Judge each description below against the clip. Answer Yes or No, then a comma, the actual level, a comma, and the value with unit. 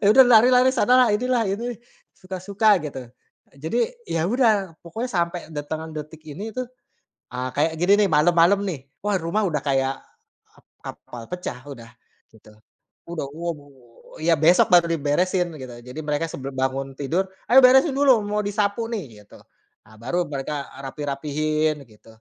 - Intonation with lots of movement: Yes, wide, 6.5 semitones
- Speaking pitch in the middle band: Yes, medium, 170 Hz